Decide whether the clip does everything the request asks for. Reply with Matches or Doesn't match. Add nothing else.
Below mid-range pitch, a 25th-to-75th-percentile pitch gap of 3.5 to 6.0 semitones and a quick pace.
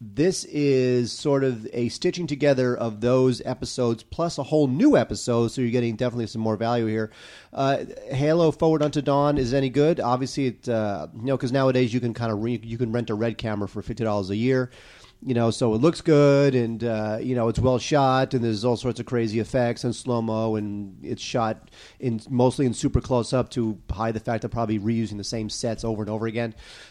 Doesn't match